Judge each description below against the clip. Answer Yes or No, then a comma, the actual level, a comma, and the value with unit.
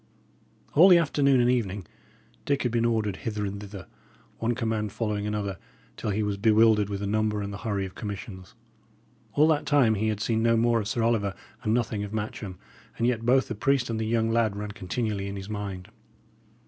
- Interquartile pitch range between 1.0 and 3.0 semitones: Yes, narrow, 2.5 semitones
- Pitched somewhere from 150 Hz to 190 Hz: No, low, 110 Hz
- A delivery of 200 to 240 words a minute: Yes, fast, 205 wpm